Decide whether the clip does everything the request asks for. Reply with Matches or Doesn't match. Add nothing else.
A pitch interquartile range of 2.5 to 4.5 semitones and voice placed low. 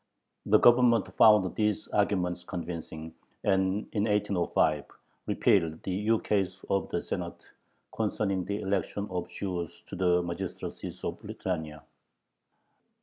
Matches